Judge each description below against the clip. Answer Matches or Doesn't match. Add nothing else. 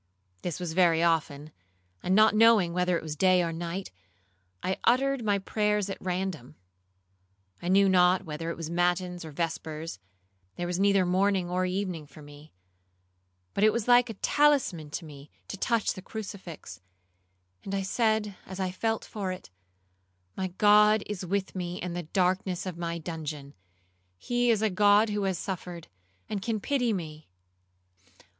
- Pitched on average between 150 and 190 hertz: Matches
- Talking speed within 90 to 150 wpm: Doesn't match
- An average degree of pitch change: Matches